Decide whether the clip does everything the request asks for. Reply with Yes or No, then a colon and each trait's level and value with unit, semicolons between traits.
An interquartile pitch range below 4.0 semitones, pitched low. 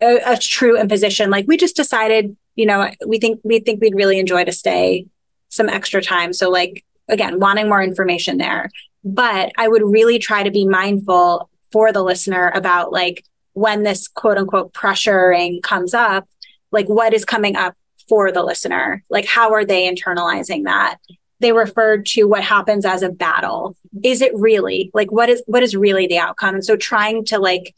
No: average, 3.1 semitones; high, 205 Hz